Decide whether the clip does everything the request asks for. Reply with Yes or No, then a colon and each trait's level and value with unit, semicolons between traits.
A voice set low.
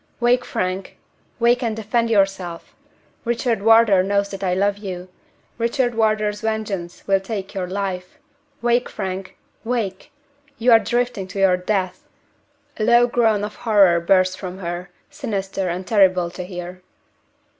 No: high, 200 Hz